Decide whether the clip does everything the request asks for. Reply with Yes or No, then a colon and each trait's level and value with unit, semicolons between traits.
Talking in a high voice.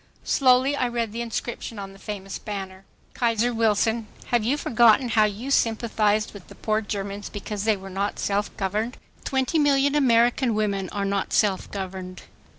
Yes: high, 215 Hz